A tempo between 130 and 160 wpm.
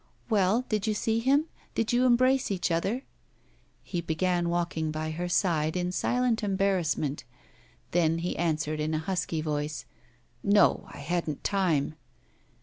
Yes: average, 145 wpm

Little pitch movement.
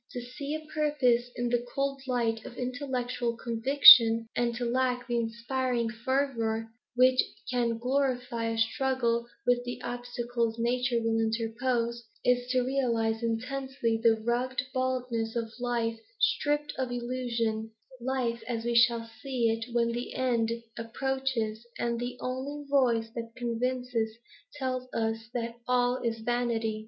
Yes: narrow, 1.9 semitones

